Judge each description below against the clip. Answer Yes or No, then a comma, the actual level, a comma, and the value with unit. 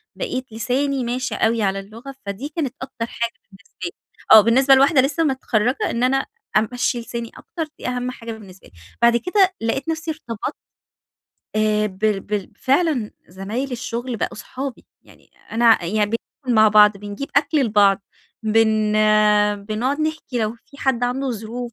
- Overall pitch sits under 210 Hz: No, high, 235 Hz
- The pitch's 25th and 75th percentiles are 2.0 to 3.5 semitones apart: No, average, 3.9 semitones